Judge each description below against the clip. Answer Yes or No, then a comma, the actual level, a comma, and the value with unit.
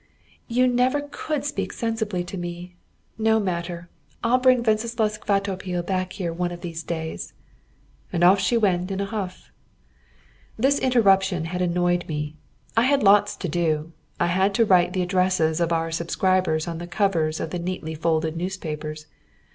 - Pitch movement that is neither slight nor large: Yes, average, 3.7 semitones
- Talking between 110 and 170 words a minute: Yes, average, 165 wpm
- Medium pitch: Yes, medium, 180 Hz